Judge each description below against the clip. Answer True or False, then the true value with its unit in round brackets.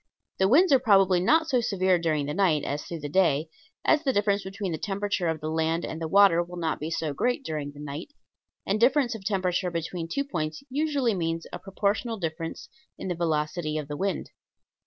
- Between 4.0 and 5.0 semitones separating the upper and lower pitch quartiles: True (4.4 semitones)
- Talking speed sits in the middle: False (210 wpm)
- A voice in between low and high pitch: True (180 Hz)